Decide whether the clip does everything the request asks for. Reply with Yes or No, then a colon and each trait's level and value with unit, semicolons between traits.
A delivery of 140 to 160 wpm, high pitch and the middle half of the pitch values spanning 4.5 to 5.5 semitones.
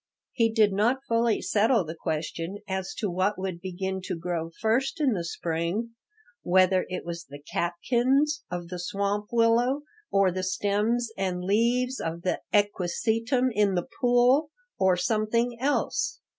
Yes: average, 150 wpm; high, 200 Hz; average, 4.8 semitones